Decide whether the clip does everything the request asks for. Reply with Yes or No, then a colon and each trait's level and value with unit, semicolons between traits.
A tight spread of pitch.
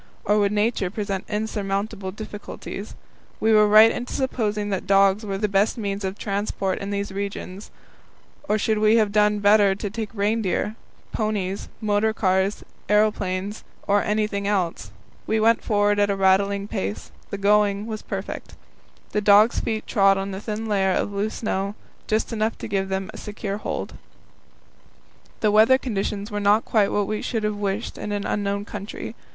Yes: narrow, 1.4 semitones